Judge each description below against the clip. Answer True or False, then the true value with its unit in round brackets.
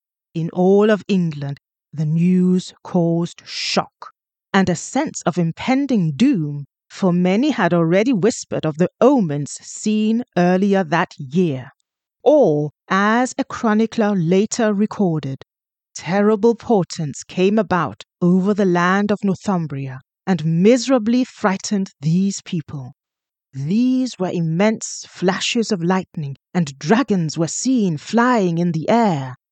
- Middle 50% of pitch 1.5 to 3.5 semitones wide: False (4.5 semitones)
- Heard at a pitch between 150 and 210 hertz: True (185 Hz)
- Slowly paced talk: True (120 wpm)